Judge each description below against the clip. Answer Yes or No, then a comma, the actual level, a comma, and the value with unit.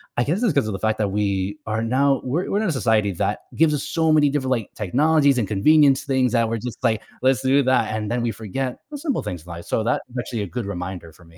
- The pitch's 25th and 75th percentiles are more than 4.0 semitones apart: Yes, average, 5.1 semitones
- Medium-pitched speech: No, low, 120 Hz